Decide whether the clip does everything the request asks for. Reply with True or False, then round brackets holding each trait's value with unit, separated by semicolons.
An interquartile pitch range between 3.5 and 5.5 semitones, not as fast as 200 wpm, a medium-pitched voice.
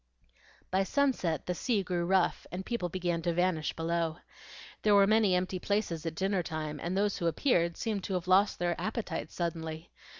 False (2.9 semitones; 180 wpm; 180 Hz)